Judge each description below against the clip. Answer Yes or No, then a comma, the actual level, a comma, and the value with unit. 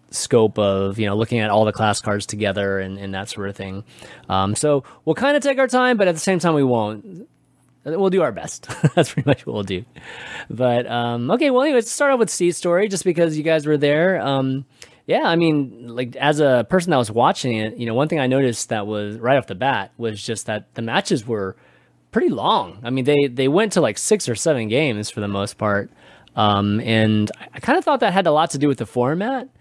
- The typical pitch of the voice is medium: No, low, 125 Hz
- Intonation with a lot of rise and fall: Yes, wide, 7.0 semitones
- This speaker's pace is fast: Yes, fast, 245 wpm